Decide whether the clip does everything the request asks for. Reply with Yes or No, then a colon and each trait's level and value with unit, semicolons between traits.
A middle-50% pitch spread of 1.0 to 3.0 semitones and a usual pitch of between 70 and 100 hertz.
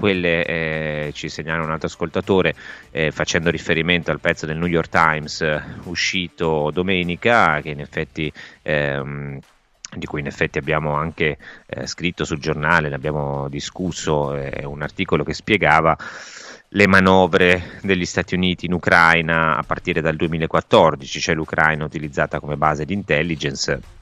Yes: narrow, 2.6 semitones; very low, 80 Hz